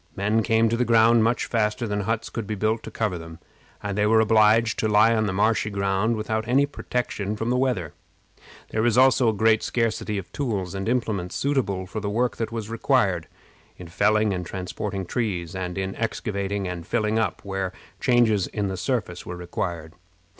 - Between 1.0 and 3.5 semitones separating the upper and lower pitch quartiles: Yes, average, 3.0 semitones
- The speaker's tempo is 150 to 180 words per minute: No, average, 195 wpm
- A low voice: Yes, low, 105 Hz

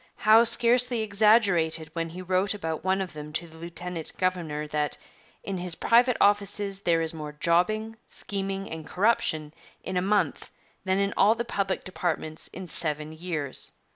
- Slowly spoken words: No, average, 165 wpm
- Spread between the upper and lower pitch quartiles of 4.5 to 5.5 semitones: No, average, 4.1 semitones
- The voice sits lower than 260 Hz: Yes, medium, 185 Hz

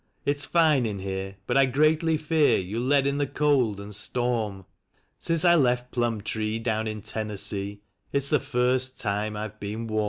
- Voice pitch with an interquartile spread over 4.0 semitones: Yes, average, 5.1 semitones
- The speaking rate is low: No, average, 180 wpm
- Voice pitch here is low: Yes, low, 120 Hz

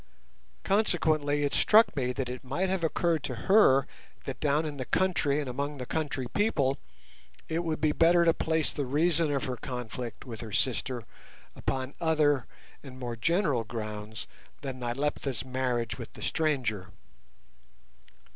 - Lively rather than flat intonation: No, average, 4.2 semitones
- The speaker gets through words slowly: No, average, 155 wpm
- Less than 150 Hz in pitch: Yes, medium, 140 Hz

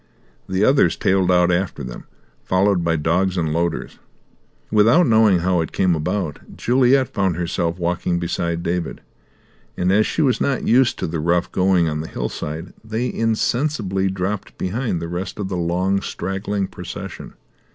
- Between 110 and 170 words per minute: Yes, average, 160 wpm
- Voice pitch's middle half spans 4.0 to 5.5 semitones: No, average, 3.4 semitones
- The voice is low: Yes, very low, 95 Hz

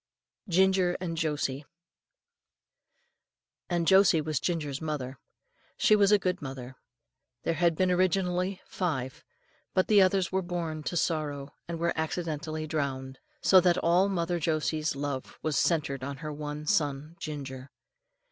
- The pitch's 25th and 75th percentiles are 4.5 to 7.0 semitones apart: No, average, 3.7 semitones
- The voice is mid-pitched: Yes, medium, 160 Hz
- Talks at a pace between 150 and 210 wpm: No, average, 140 wpm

